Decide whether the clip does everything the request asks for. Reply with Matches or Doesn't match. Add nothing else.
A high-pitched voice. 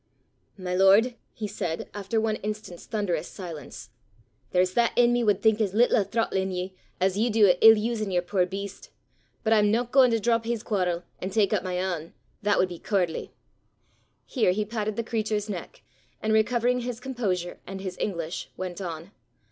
Matches